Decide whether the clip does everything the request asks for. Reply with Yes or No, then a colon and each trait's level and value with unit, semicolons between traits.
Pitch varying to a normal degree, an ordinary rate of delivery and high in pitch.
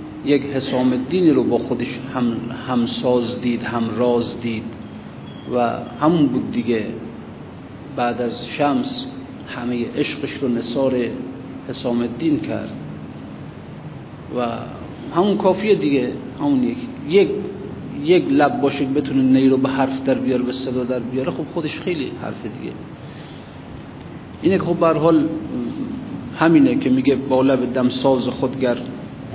No: average, 3.0 semitones; average, 130 wpm; low, 130 Hz